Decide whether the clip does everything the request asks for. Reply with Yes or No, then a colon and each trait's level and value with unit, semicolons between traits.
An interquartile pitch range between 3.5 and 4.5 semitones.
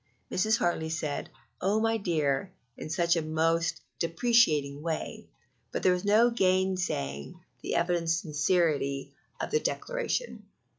Yes: average, 4.0 semitones